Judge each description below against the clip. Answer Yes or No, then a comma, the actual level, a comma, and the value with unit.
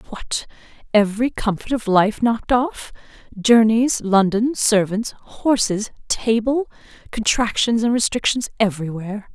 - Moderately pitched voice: No, high, 220 Hz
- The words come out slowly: Yes, slow, 105 wpm